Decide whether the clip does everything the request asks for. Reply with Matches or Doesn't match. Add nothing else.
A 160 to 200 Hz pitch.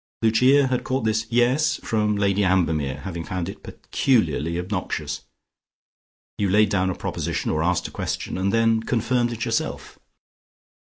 Doesn't match